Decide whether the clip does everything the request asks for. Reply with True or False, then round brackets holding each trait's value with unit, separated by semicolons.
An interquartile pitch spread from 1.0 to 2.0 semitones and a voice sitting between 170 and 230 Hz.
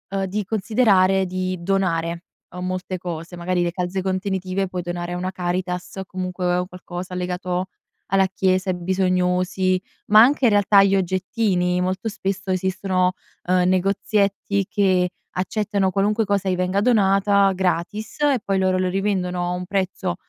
True (1.5 semitones; 185 Hz)